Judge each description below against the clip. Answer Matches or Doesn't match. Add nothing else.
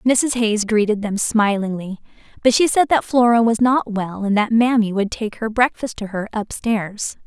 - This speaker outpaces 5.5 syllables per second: Doesn't match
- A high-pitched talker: Matches